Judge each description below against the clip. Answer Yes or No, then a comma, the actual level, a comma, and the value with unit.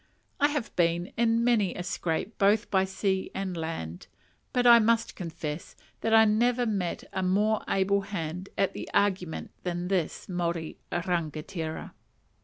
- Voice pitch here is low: No, high, 190 Hz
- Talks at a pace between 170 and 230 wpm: No, average, 150 wpm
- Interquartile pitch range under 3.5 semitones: No, average, 4.0 semitones